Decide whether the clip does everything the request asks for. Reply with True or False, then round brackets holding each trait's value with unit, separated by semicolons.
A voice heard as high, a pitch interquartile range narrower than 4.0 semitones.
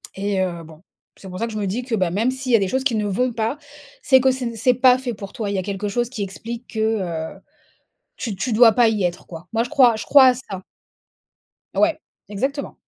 False (225 Hz; 4.3 semitones)